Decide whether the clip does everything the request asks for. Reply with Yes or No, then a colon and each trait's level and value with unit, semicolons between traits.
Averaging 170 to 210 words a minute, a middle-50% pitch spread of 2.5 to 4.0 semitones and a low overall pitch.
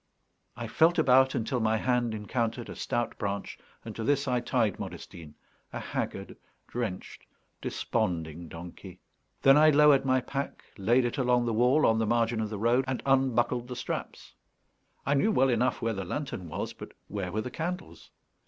Yes: average, 175 wpm; average, 3.5 semitones; low, 120 Hz